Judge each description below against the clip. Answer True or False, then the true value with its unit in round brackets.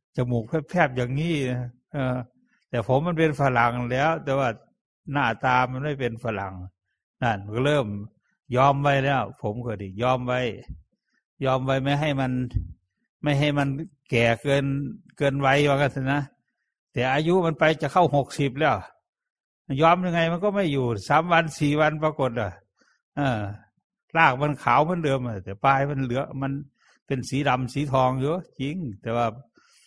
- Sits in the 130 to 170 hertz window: True (135 Hz)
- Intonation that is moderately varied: True (3.4 semitones)